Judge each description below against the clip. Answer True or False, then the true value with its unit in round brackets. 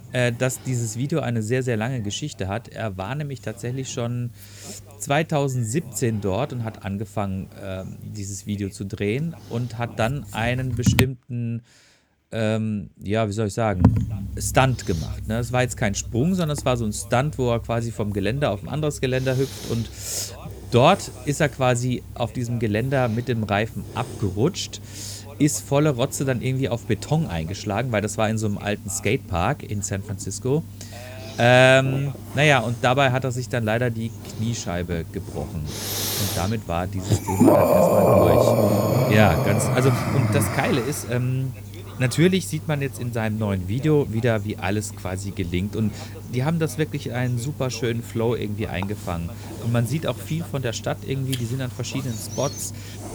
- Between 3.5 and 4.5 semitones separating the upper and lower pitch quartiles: True (3.8 semitones)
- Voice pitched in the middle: False (115 Hz)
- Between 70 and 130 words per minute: False (175 wpm)